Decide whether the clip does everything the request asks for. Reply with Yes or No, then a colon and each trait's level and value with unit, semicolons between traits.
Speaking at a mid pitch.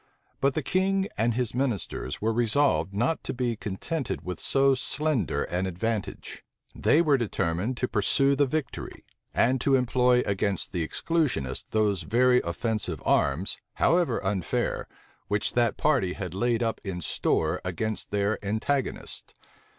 No: low, 115 Hz